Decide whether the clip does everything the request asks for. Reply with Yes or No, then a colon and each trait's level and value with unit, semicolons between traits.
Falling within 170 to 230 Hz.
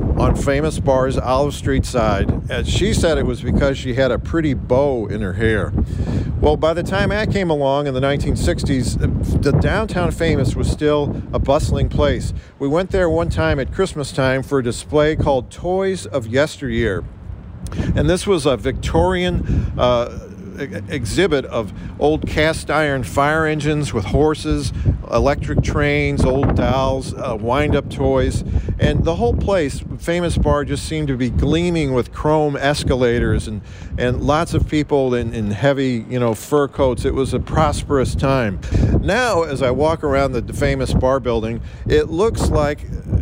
No: low, 135 Hz